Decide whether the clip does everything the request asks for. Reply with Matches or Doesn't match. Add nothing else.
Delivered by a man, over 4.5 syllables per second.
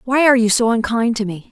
Doesn't match